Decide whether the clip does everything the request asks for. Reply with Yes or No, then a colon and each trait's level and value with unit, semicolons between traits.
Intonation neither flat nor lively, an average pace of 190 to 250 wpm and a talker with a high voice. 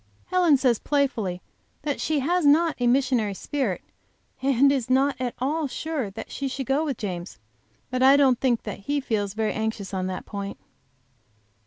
No: average, 4.6 semitones; average, 175 wpm; very high, 260 Hz